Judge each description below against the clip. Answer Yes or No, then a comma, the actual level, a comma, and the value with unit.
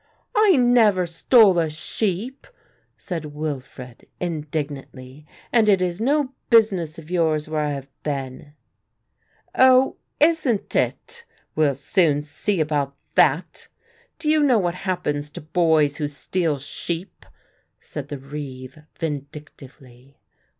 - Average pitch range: No, wide, 5.8 semitones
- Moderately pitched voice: Yes, medium, 160 Hz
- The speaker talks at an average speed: No, slow, 120 wpm